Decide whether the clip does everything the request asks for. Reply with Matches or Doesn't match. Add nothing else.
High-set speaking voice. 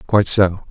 Doesn't match